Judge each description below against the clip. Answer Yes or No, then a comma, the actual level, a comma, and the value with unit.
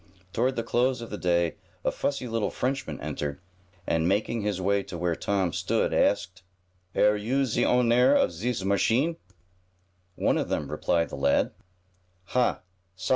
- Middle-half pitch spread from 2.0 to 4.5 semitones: No, wide, 5.6 semitones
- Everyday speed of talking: Yes, average, 155 wpm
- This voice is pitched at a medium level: No, low, 105 Hz